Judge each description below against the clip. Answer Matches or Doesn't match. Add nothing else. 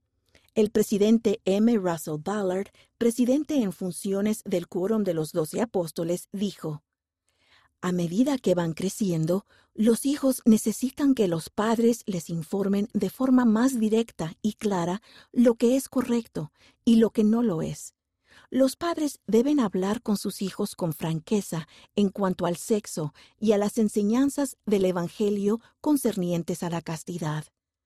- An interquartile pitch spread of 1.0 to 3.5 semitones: Doesn't match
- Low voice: Doesn't match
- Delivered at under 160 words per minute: Matches